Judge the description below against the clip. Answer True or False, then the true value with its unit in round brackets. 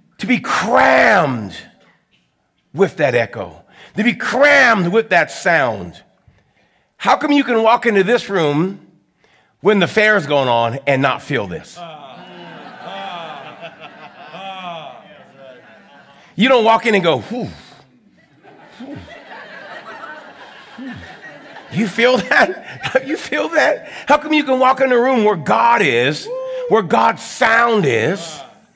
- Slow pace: True (125 wpm)